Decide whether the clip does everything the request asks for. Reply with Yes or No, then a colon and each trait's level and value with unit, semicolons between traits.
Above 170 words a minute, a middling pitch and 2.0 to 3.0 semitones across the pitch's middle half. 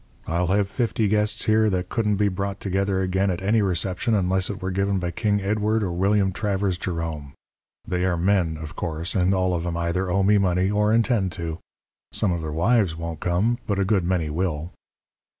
No: fast, 205 wpm; very low, 95 Hz; average, 2.7 semitones